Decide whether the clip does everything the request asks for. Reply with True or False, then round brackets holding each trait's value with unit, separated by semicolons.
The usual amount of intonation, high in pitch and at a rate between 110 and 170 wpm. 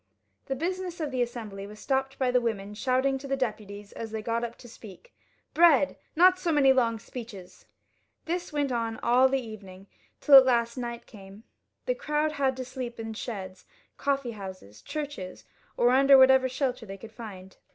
False (4.0 semitones; 245 Hz; 185 wpm)